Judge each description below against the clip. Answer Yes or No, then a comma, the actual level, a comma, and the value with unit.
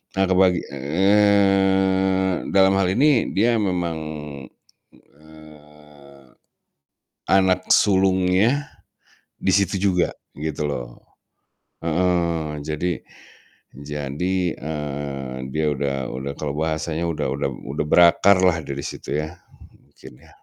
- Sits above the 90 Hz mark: No, very low, 85 Hz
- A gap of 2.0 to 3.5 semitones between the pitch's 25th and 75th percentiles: No, average, 4.4 semitones